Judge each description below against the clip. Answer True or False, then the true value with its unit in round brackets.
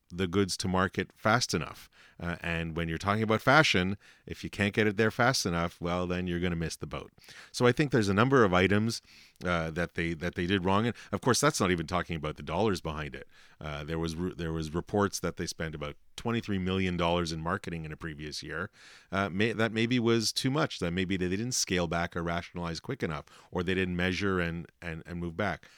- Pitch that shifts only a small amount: False (3.2 semitones)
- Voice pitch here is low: True (90 Hz)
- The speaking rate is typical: False (235 wpm)